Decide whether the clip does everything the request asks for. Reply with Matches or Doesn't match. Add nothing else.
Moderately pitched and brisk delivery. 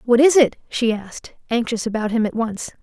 Doesn't match